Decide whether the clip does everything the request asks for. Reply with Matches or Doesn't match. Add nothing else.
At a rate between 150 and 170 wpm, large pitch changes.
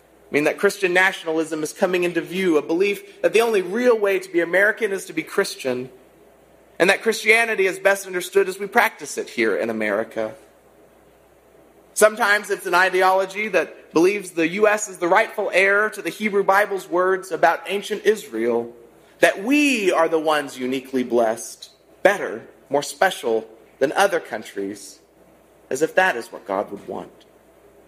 Matches